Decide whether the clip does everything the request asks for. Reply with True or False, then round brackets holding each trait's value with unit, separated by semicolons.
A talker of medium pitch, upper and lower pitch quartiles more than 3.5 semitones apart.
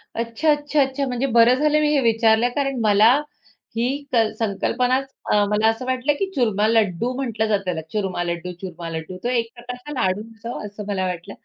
False (230 Hz; 3.9 semitones)